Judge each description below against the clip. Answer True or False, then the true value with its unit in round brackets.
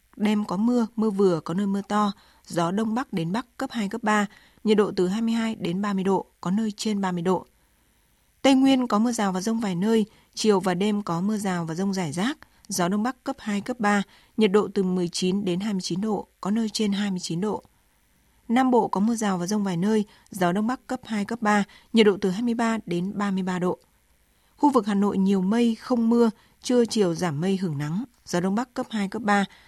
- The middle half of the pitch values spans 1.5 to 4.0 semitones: True (2.9 semitones)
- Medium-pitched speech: False (205 Hz)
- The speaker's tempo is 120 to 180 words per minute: False (225 wpm)